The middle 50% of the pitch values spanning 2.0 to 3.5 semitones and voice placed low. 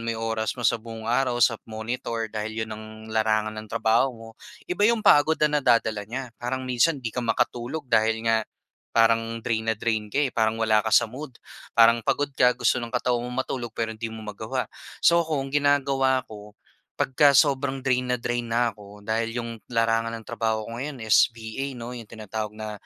Yes: average, 2.7 semitones; low, 115 Hz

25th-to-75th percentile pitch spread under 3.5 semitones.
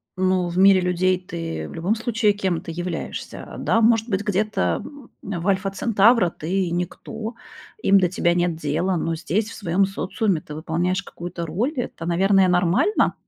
Yes: average, 2.9 semitones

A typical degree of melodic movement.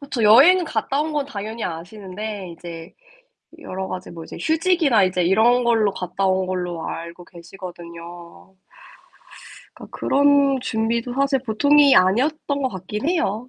No: wide, 7.0 semitones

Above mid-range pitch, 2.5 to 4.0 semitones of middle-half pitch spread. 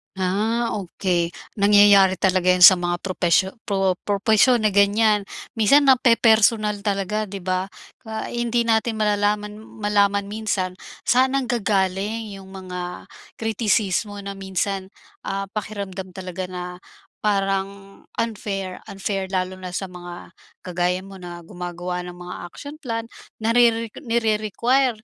Yes: high, 200 Hz; average, 2.8 semitones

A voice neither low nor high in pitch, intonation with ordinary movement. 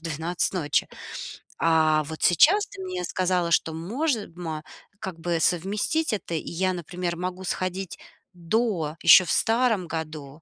Yes: medium, 175 Hz; average, 3.4 semitones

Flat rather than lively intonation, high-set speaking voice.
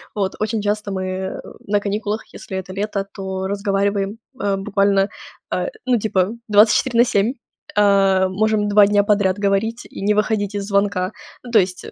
Yes: narrow, 1.4 semitones; high, 200 Hz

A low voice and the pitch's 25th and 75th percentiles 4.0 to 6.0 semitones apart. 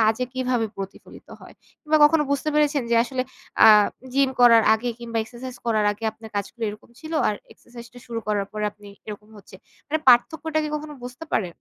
No: high, 240 Hz; average, 4.3 semitones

